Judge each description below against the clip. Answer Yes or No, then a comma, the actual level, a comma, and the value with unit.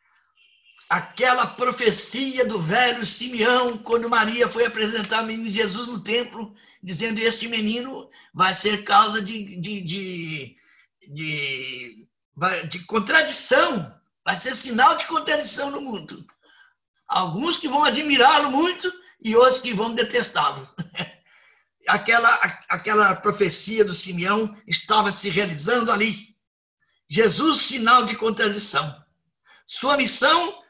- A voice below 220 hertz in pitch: No, high, 225 Hz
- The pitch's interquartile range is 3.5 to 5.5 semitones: Yes, average, 4.0 semitones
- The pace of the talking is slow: Yes, slow, 115 wpm